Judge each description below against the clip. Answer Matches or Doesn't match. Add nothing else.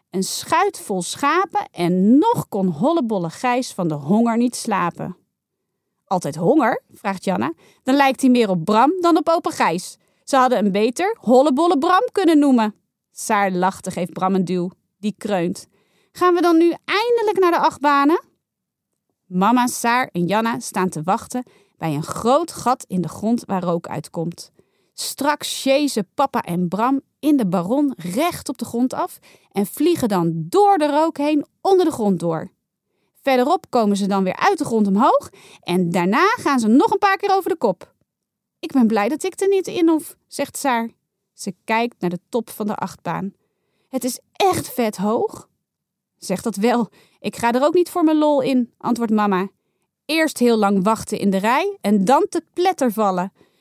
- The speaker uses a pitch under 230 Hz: Doesn't match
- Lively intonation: Matches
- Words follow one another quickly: Doesn't match